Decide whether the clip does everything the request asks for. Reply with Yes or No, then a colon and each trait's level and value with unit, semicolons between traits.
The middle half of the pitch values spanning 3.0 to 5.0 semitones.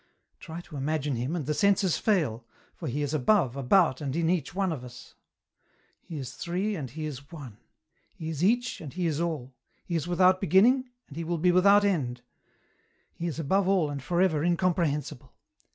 Yes: average, 4.5 semitones